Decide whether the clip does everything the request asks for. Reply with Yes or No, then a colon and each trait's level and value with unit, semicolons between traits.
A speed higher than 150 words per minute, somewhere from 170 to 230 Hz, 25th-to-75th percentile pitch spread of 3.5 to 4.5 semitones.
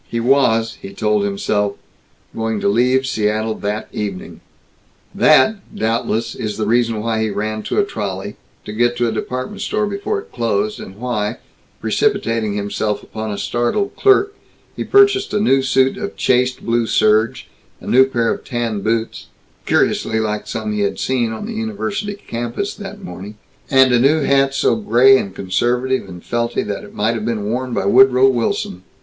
No: average, 175 wpm; low, 115 Hz; average, 3.8 semitones